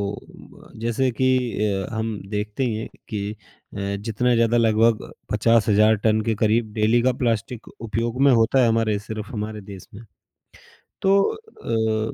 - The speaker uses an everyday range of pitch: No, narrow, 1.7 semitones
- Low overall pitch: Yes, low, 110 Hz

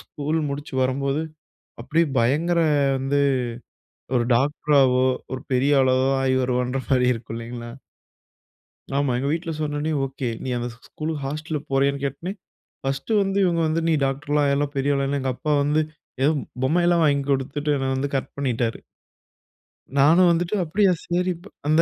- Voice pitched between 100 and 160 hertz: Yes, medium, 140 Hz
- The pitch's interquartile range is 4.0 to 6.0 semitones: No, average, 3.0 semitones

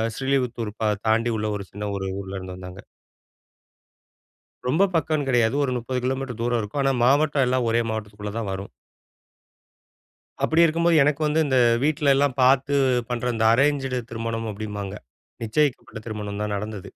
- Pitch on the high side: No, low, 120 Hz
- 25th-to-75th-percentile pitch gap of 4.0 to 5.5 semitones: Yes, average, 4.6 semitones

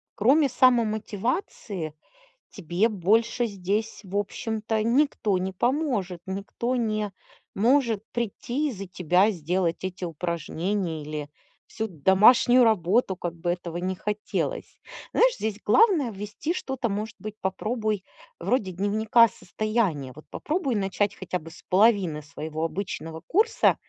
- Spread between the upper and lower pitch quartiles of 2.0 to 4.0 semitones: No, average, 4.5 semitones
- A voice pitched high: Yes, high, 205 Hz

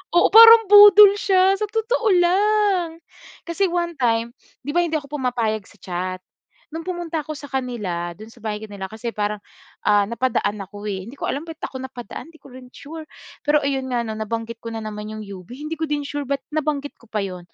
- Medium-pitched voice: No, very high, 270 Hz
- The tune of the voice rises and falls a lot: Yes, wide, 7.3 semitones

